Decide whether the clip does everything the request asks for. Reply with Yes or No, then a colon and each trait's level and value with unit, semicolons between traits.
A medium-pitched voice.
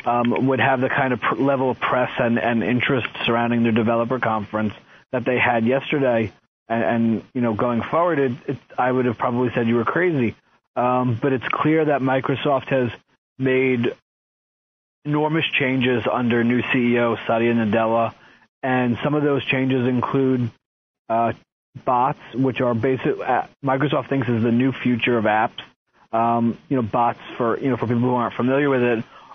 No: low, 125 Hz